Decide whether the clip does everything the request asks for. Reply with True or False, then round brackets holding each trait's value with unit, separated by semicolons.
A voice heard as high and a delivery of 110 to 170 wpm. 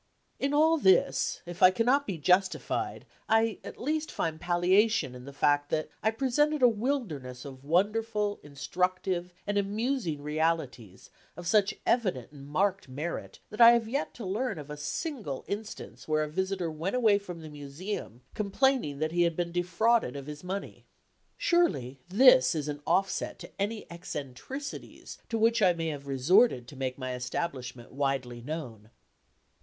False (175 Hz; 160 wpm)